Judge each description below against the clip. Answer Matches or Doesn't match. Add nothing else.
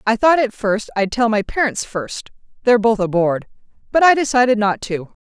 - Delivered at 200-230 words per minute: Doesn't match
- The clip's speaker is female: Matches